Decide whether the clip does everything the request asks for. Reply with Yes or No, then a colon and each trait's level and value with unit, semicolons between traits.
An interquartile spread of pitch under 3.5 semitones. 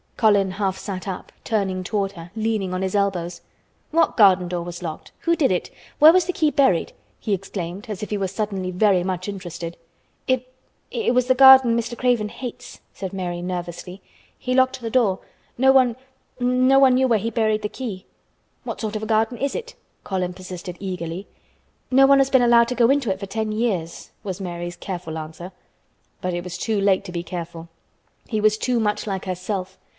No: average, 5.1 semitones